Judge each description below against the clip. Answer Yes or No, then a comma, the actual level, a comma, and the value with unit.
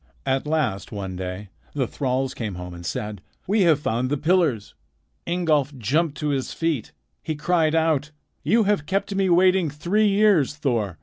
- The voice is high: No, medium, 150 Hz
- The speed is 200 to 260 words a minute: No, average, 170 wpm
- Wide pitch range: Yes, wide, 6.6 semitones